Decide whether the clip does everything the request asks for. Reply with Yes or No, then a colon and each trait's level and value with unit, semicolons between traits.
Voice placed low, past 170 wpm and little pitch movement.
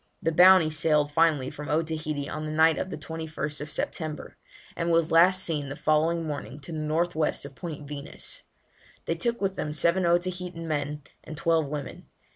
No: medium, 155 Hz; average, 180 wpm; narrow, 2.0 semitones